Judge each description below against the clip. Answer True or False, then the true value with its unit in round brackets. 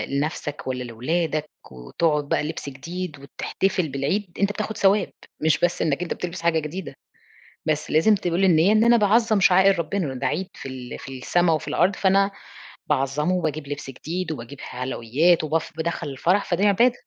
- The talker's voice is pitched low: False (165 Hz)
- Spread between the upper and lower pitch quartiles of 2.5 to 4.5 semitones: False (4.9 semitones)